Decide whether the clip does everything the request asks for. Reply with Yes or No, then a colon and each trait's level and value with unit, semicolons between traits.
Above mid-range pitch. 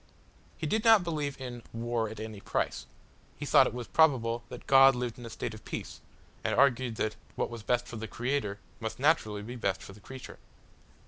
No: low, 120 Hz